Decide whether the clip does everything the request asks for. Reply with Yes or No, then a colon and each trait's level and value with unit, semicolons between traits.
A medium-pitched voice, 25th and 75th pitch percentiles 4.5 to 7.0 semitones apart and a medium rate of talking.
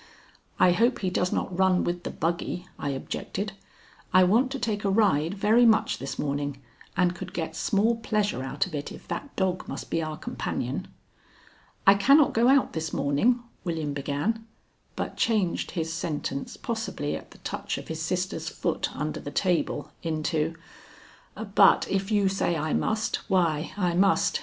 Yes: medium, 180 Hz; average, 4.8 semitones; average, 170 wpm